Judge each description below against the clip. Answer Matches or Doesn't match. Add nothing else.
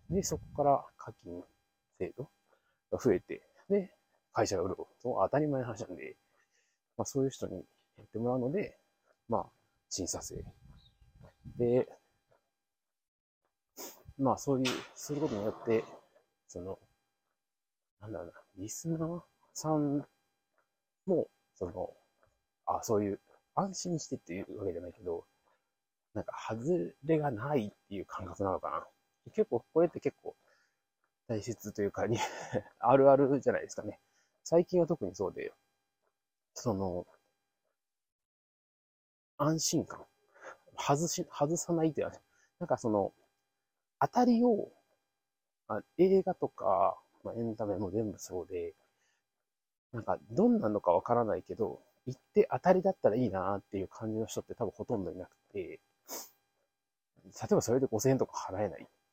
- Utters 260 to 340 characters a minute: Matches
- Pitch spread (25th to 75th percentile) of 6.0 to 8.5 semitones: Matches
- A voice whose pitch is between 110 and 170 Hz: Matches